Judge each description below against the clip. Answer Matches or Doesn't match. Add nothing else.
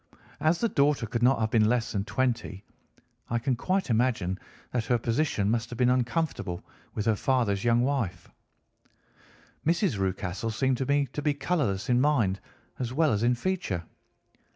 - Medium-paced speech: Matches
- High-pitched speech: Doesn't match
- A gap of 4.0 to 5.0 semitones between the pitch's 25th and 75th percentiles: Matches